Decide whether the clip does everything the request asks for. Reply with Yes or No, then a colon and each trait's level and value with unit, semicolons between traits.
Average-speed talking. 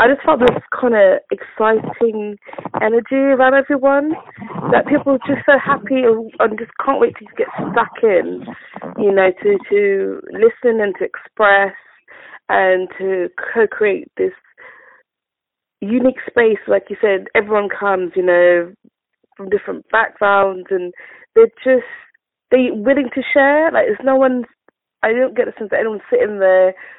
Yes: average, 155 wpm